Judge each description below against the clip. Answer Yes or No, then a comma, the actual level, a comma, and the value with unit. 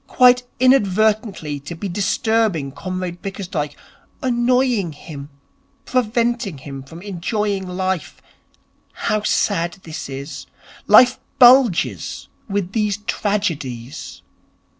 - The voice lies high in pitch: Yes, high, 195 Hz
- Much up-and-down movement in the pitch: Yes, wide, 5.7 semitones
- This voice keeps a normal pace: No, slow, 95 wpm